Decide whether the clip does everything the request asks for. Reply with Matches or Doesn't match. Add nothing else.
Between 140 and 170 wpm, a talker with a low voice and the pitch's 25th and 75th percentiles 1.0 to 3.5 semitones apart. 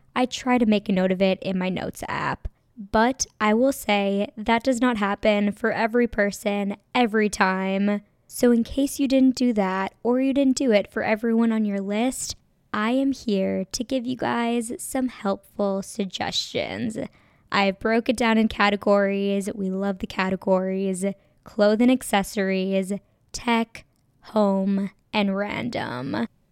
Doesn't match